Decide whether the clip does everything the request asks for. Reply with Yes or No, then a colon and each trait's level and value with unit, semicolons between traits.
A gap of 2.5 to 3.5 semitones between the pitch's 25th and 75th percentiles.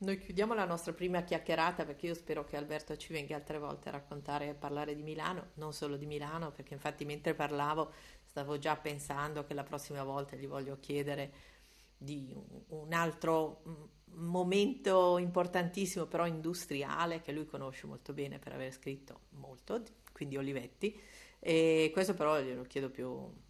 Yes: average, 2.8 semitones